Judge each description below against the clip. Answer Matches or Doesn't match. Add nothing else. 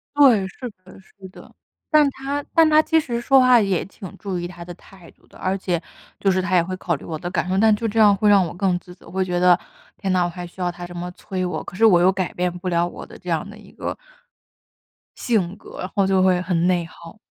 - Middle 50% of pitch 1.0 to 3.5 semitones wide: Matches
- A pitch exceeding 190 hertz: Doesn't match